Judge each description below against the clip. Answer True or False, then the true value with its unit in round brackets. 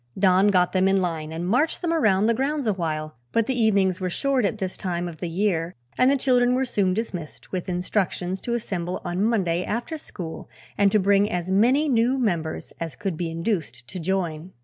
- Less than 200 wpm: False (205 wpm)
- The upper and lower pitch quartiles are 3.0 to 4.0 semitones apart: False (4.6 semitones)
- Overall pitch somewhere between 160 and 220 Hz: True (190 Hz)